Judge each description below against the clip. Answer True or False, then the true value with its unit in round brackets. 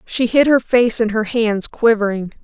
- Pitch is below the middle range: False (225 Hz)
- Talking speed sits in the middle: True (195 wpm)